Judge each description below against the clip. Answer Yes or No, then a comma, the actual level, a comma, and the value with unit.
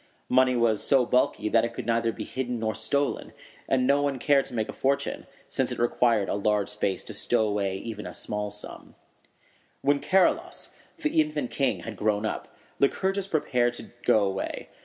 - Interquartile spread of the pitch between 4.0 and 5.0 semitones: Yes, average, 4.6 semitones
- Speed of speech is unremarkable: Yes, average, 185 wpm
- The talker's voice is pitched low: Yes, low, 120 Hz